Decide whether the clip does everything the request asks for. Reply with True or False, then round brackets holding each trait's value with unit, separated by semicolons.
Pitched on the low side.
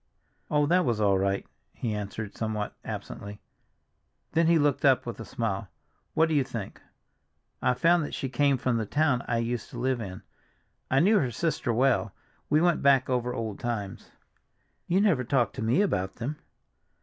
True (125 Hz)